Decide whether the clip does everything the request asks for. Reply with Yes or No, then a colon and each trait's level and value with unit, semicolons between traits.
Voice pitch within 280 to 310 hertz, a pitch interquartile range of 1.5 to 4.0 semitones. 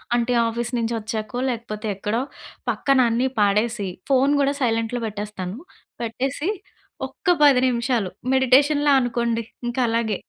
No: high, 235 Hz; average, 2.8 semitones